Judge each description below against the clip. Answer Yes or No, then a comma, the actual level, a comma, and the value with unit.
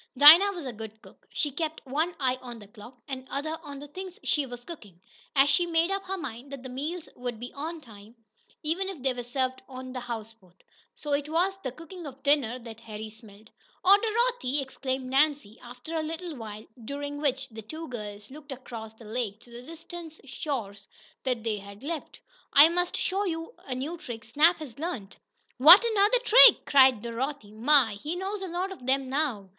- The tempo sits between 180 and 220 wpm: Yes, average, 200 wpm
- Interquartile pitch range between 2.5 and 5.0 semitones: No, wide, 5.5 semitones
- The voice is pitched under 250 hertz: No, very high, 270 Hz